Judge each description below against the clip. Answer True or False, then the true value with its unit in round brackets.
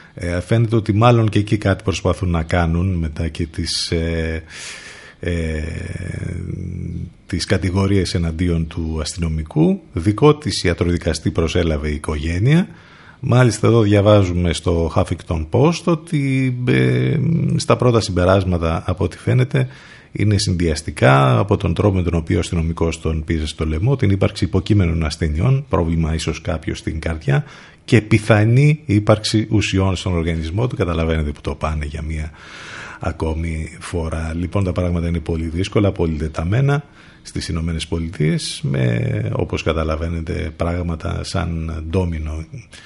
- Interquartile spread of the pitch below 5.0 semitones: True (4.4 semitones)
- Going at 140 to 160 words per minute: False (130 wpm)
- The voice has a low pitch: True (90 Hz)